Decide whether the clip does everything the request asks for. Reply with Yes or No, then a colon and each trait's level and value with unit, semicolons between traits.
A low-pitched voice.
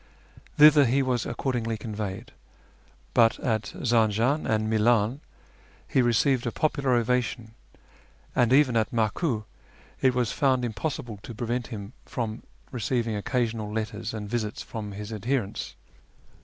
Yes: low, 115 Hz